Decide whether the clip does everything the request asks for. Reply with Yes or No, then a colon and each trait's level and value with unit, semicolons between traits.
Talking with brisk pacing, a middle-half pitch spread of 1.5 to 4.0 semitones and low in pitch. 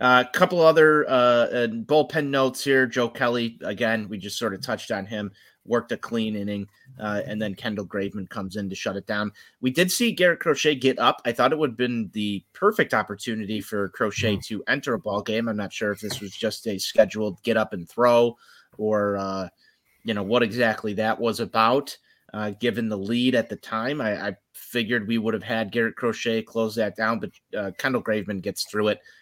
Yes: fast, 215 wpm; average, 2.9 semitones; low, 110 Hz